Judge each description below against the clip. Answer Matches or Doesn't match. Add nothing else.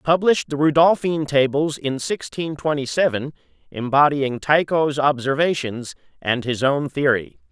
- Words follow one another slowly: Matches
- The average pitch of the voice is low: Doesn't match